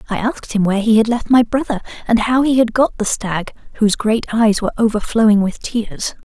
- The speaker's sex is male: No, female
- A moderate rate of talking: No, fast, 220 wpm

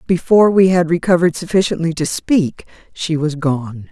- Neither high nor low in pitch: Yes, medium, 165 Hz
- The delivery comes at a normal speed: Yes, average, 155 wpm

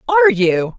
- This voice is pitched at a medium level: Yes, medium, 160 Hz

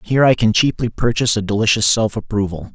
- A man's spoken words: Yes, male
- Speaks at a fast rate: No, average, 195 wpm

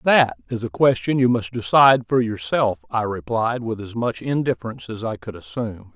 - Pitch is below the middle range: Yes, low, 115 Hz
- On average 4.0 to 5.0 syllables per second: No, 5.4 syllables/s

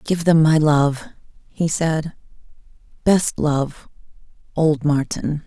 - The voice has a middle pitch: Yes, medium, 155 Hz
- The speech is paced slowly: Yes, slow, 100 wpm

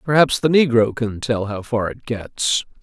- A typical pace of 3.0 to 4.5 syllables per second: Yes, 4.3 syllables/s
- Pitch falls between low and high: No, low, 120 Hz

